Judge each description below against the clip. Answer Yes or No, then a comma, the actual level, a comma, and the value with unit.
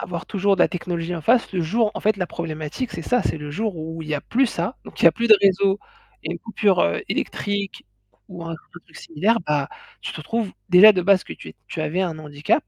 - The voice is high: No, medium, 180 Hz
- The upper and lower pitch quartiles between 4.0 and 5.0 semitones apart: Yes, average, 4.3 semitones